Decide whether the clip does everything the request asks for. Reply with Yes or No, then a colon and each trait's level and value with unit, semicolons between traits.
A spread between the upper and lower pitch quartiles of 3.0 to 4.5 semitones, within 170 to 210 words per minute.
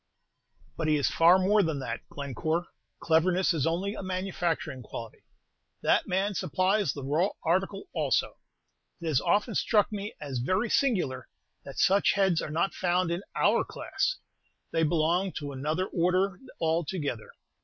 No: average, 3.9 semitones; average, 150 wpm